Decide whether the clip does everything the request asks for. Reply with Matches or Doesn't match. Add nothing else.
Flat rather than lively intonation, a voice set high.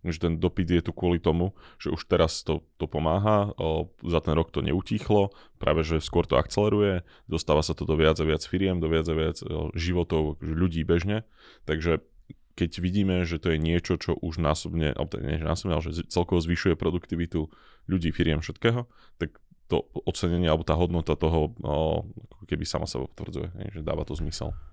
Doesn't match